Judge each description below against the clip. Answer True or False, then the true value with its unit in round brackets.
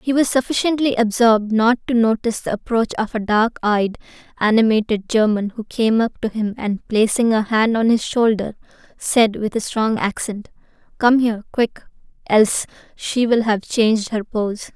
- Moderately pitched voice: False (220 Hz)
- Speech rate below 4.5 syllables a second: False (4.9 syllables/s)